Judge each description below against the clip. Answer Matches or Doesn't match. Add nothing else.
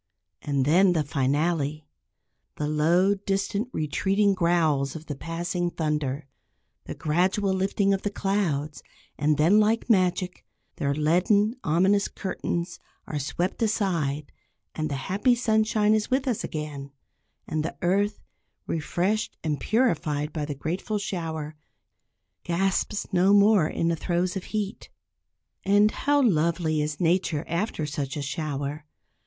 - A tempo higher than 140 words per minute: Doesn't match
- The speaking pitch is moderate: Matches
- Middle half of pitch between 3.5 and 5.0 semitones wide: Matches